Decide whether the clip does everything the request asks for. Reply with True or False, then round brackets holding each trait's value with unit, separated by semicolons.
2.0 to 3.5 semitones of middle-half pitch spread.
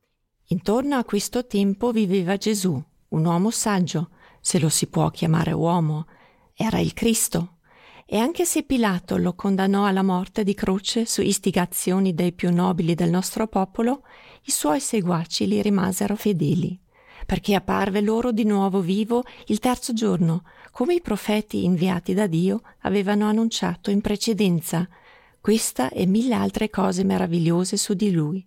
True (3.2 semitones)